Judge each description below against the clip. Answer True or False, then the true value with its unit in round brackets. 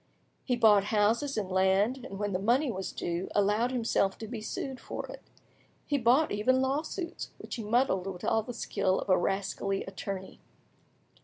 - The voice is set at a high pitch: True (215 Hz)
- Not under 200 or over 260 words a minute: False (175 wpm)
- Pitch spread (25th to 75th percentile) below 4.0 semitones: False (4.6 semitones)